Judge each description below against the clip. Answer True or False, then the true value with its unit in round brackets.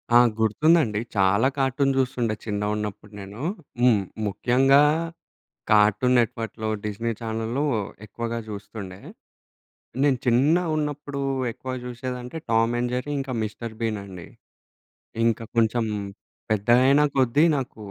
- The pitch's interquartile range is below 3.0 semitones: False (3.7 semitones)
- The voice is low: True (115 Hz)